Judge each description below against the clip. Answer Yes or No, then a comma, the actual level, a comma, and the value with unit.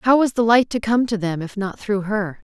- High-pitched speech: Yes, high, 215 Hz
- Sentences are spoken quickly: Yes, fast, 285 wpm